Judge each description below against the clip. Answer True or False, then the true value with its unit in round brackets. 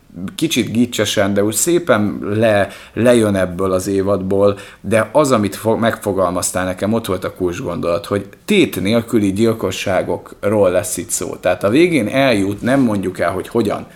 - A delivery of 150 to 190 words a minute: True (155 wpm)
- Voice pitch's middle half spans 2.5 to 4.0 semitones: True (2.8 semitones)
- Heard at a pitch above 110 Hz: False (105 Hz)